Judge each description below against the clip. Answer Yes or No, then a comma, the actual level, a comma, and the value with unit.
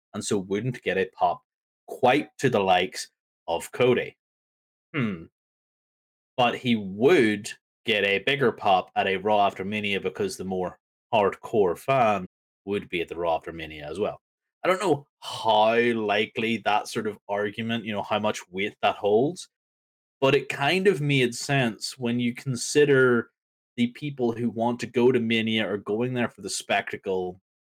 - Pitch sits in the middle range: No, low, 115 Hz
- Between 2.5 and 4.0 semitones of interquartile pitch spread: Yes, average, 3.5 semitones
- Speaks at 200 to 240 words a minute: No, average, 170 wpm